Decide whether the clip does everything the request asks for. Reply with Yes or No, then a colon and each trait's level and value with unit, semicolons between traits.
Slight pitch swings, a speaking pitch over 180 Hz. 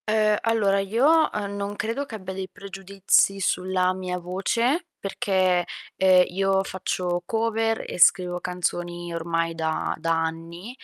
No: average, 3.0 semitones; high, 190 Hz